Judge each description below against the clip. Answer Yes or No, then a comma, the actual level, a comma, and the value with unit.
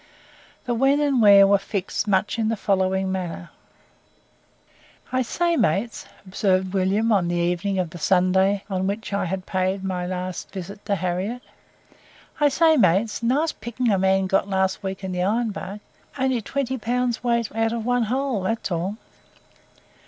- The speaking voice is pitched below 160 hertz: No, high, 200 Hz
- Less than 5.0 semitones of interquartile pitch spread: Yes, average, 3.9 semitones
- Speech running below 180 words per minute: Yes, average, 170 wpm